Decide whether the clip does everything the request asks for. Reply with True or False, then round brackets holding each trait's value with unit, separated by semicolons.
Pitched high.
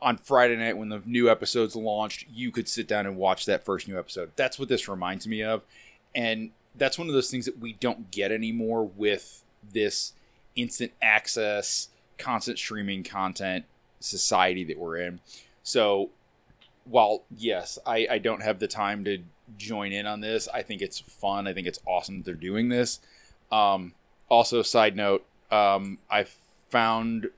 False (110 Hz)